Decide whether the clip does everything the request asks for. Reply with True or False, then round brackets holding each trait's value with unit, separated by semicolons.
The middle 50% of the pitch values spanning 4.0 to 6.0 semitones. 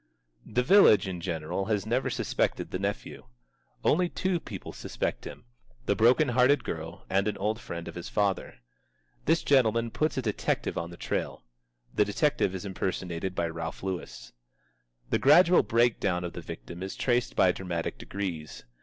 True (5.6 semitones)